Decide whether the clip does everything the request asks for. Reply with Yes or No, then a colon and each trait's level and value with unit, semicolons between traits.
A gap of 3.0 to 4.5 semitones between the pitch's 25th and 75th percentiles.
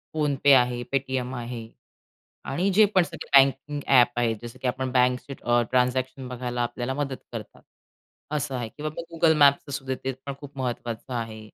No: narrow, 2.4 semitones